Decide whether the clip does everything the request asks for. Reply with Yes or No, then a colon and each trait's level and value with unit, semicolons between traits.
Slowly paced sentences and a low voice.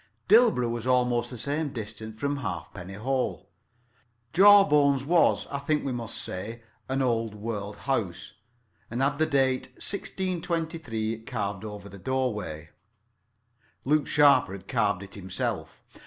Yes: slow, 130 wpm; low, 125 Hz